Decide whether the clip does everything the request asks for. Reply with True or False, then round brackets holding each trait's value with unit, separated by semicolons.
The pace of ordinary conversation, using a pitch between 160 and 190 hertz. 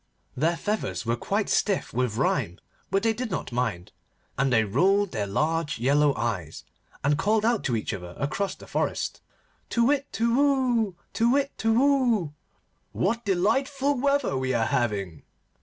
True (160 wpm; 185 Hz)